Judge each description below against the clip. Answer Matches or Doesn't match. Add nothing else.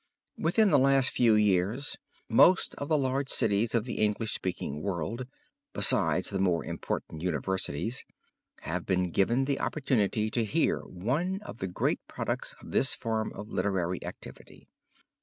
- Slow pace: Doesn't match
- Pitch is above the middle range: Doesn't match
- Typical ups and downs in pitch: Doesn't match